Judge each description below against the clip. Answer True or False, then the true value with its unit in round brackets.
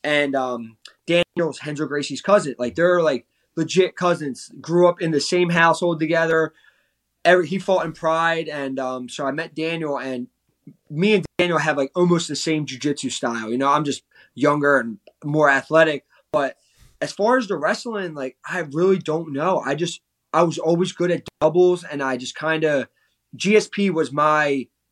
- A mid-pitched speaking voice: True (155 Hz)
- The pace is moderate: True (180 wpm)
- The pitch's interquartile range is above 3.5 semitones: True (3.9 semitones)